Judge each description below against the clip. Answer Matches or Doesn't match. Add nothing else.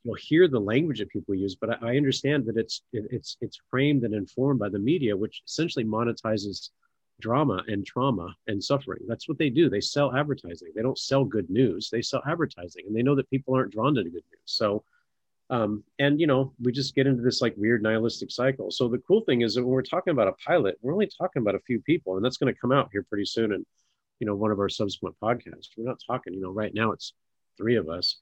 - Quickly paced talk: Matches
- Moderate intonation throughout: Matches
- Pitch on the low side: Matches